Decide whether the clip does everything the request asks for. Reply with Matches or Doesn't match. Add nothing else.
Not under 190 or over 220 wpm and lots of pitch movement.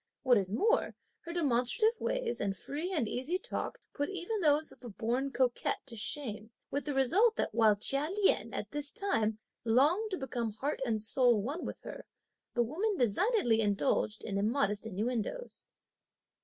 Doesn't match